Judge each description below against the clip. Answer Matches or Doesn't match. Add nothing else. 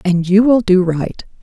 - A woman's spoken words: Matches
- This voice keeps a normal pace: Doesn't match